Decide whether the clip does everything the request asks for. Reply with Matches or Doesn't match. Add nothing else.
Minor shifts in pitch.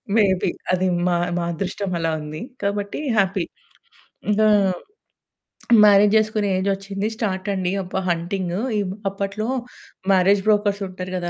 Matches